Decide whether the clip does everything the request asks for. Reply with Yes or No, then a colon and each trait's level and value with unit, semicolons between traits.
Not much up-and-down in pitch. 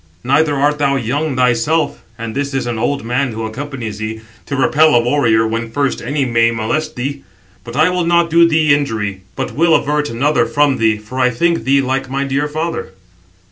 No: average, 4.2 semitones